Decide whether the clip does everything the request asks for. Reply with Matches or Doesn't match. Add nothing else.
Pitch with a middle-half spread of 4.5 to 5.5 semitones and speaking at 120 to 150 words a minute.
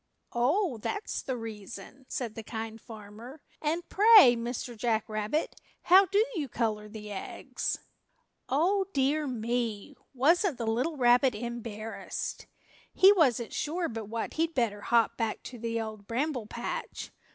Matches